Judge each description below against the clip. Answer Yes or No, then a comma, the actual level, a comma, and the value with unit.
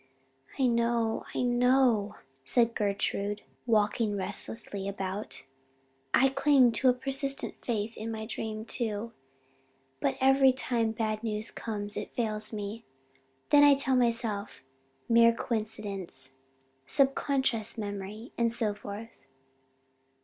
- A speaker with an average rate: No, slow, 115 wpm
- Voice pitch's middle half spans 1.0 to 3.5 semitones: Yes, average, 2.9 semitones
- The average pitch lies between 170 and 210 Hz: No, high, 225 Hz